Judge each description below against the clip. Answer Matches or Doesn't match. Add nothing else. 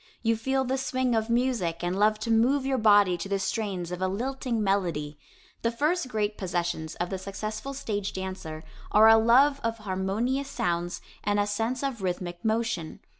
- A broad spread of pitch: Doesn't match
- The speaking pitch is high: Matches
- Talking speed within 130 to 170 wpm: Doesn't match